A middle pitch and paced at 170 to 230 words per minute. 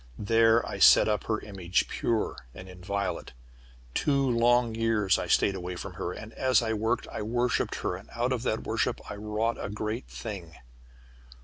No: low, 110 Hz; average, 180 wpm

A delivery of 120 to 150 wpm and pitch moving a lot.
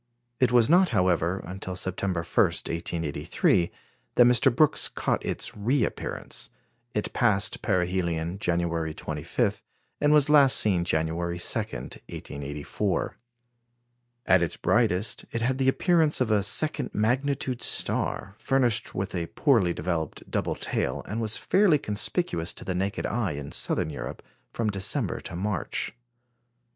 Yes: slow, 135 wpm; wide, 6.1 semitones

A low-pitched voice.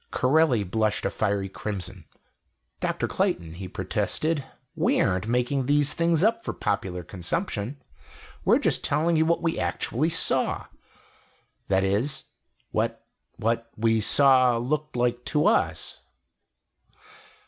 Yes: low, 120 Hz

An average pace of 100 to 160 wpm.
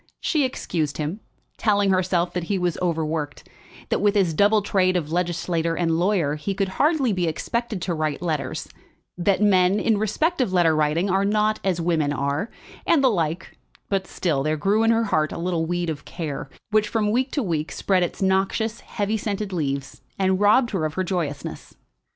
No: average, 190 wpm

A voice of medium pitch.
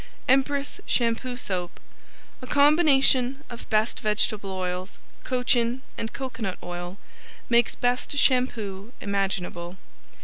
No: high, 235 Hz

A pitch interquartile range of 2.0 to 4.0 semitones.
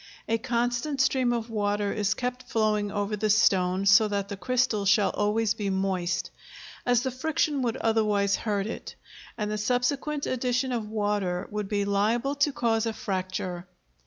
Yes: average, 3.3 semitones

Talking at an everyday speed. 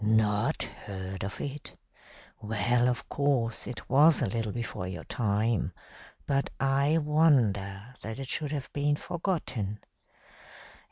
No: slow, 125 wpm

